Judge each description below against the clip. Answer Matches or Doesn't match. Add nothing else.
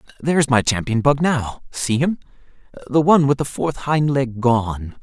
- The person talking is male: Matches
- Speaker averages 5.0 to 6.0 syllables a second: Doesn't match